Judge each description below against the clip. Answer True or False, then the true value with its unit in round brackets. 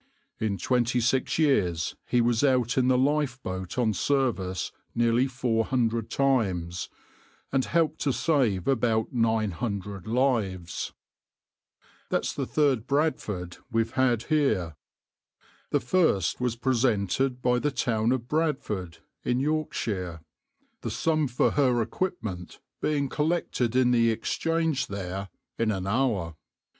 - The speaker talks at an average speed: False (125 wpm)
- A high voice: False (120 Hz)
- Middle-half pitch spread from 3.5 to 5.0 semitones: True (4.7 semitones)